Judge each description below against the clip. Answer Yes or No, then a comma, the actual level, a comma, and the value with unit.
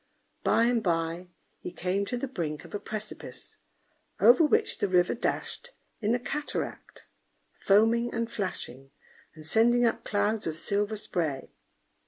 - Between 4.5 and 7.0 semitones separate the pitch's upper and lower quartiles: Yes, average, 4.9 semitones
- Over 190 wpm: No, average, 145 wpm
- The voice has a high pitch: Yes, high, 210 Hz